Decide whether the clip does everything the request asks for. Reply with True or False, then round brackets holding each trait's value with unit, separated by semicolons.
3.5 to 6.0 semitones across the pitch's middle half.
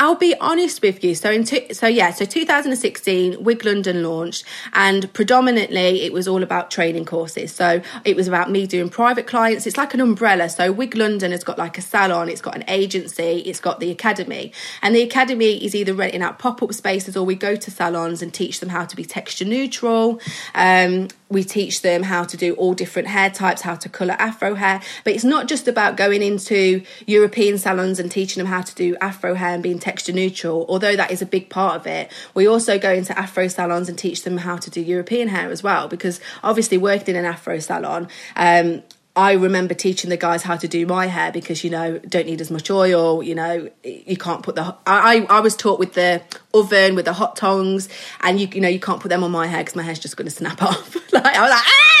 False (2.8 semitones)